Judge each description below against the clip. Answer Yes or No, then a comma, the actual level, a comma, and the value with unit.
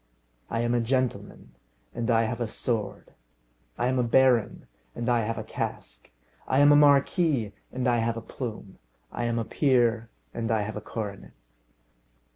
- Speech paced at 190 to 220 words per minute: No, average, 175 wpm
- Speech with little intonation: Yes, narrow, 2.2 semitones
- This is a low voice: Yes, low, 120 Hz